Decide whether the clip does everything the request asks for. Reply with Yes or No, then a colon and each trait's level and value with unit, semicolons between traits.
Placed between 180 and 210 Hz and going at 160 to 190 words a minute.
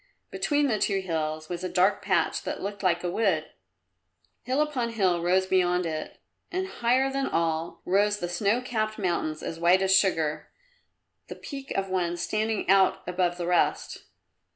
Yes: high, 190 Hz; average, 170 wpm